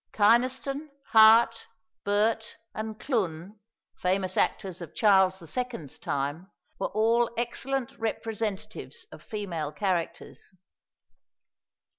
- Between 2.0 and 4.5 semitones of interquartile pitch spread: Yes, average, 3.8 semitones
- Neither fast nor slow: No, slow, 90 wpm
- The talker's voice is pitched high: Yes, high, 215 Hz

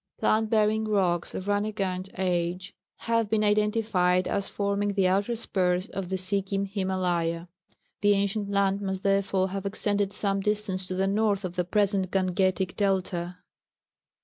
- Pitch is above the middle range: Yes, high, 195 Hz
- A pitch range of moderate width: No, narrow, 1.8 semitones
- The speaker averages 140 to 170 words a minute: Yes, average, 150 wpm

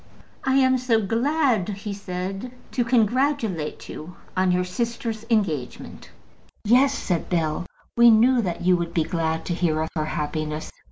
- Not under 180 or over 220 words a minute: No, average, 155 wpm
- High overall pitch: Yes, high, 195 Hz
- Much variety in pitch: Yes, wide, 6.0 semitones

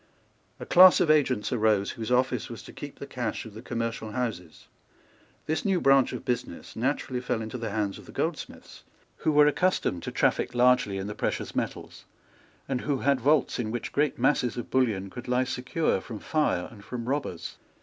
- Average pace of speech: Yes, average, 190 wpm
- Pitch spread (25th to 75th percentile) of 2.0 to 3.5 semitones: No, average, 3.9 semitones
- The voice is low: Yes, low, 125 Hz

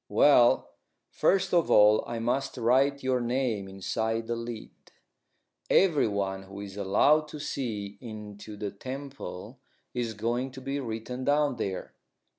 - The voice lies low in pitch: Yes, low, 120 Hz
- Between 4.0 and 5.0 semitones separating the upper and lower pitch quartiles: Yes, average, 4.6 semitones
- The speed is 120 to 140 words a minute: Yes, slow, 135 wpm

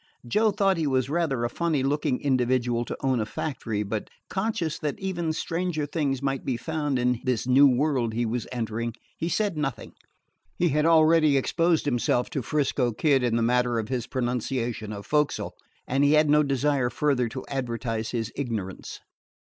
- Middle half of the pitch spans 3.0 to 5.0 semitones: Yes, average, 4.1 semitones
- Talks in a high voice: No, low, 135 Hz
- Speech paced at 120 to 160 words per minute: No, average, 180 wpm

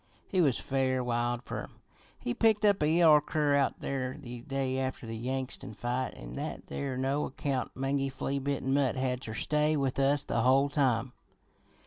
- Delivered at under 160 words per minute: No, average, 185 wpm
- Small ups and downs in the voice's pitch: Yes, narrow, 2.0 semitones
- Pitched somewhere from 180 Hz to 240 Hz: No, low, 135 Hz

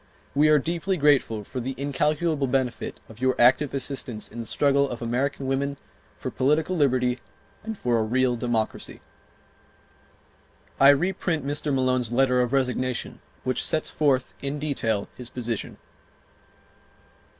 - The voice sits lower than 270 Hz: Yes, low, 135 Hz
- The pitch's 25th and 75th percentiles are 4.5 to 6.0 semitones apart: No, average, 2.7 semitones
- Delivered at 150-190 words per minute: No, average, 140 wpm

